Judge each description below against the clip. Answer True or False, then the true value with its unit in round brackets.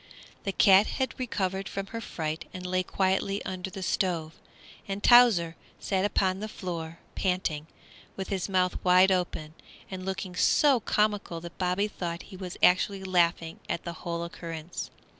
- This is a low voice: False (185 Hz)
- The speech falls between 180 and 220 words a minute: False (160 wpm)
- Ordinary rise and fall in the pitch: False (2.3 semitones)